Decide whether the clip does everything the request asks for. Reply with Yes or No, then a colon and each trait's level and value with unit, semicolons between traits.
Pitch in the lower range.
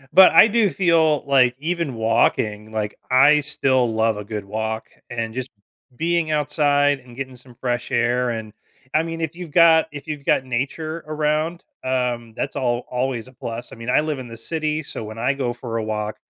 Yes: low, 130 Hz